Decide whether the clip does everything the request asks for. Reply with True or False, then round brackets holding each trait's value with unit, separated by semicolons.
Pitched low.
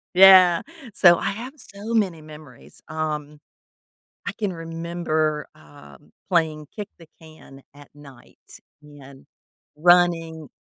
False (160 Hz)